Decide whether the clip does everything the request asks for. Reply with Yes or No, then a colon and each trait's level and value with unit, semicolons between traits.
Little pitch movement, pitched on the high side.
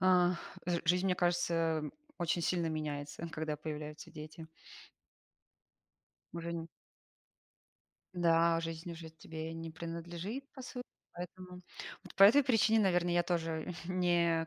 No: narrow, 1.8 semitones; medium, 170 Hz